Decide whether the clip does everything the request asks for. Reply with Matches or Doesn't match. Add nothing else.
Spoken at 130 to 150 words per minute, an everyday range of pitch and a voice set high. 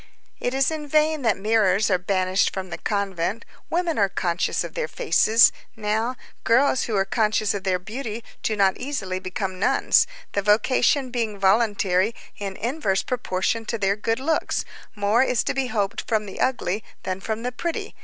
Doesn't match